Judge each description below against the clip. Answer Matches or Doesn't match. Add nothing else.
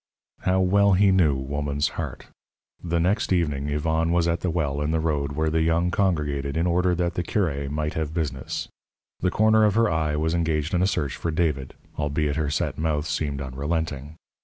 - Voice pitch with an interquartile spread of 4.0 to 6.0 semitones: Doesn't match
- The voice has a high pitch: Doesn't match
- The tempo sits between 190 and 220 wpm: Matches